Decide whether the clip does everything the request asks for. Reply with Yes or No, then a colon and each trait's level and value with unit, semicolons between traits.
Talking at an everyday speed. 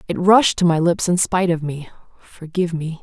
No: fast, 220 wpm